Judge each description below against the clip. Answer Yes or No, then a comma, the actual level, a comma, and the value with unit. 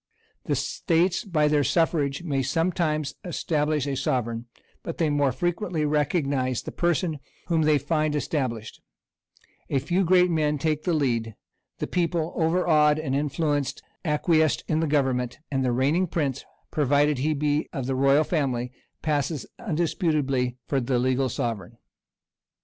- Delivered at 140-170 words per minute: Yes, average, 145 wpm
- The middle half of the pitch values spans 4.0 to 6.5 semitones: No, average, 3.3 semitones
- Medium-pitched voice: Yes, medium, 150 Hz